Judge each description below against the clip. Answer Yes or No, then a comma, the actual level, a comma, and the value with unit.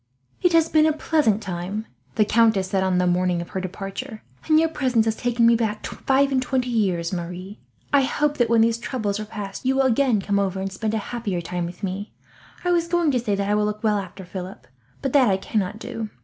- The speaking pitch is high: Yes, high, 215 Hz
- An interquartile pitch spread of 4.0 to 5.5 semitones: Yes, average, 5.0 semitones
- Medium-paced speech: No, fast, 235 wpm